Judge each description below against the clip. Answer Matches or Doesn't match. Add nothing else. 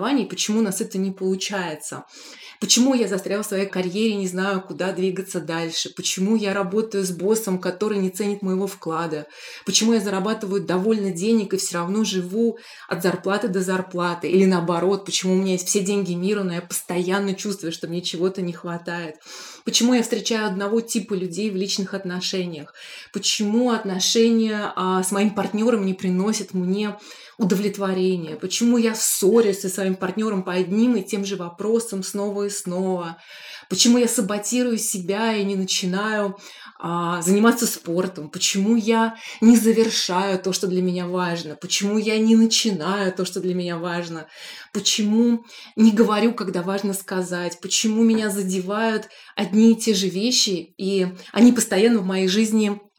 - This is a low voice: Doesn't match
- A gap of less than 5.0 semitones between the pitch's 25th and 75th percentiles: Matches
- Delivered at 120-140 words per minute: Doesn't match